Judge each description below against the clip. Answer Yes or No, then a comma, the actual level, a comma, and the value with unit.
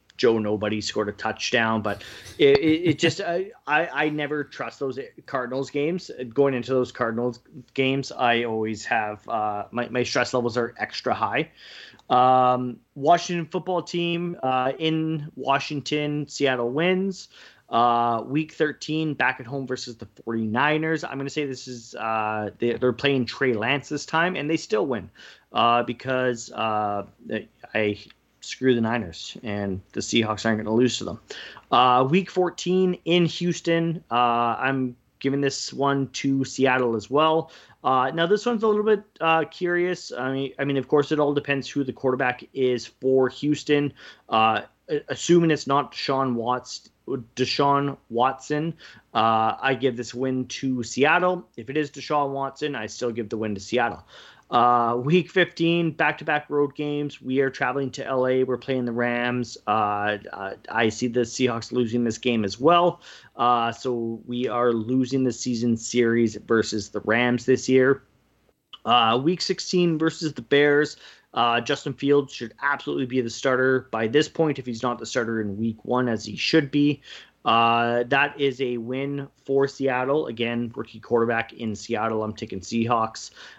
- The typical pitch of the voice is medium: No, low, 130 Hz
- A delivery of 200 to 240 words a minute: No, average, 165 wpm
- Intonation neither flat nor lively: Yes, average, 3.8 semitones